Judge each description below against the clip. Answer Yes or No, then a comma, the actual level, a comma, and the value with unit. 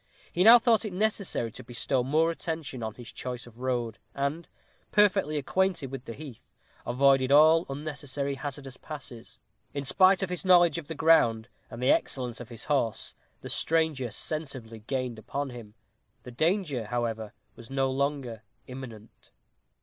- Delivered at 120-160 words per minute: Yes, average, 155 wpm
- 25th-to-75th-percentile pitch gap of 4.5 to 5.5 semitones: Yes, average, 4.8 semitones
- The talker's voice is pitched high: No, low, 135 Hz